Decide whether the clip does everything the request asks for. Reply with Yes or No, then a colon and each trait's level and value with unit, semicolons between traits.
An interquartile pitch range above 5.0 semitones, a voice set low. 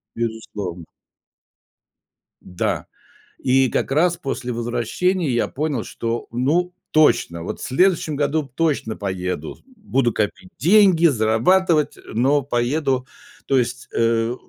Yes: wide, 5.4 semitones; low, 130 Hz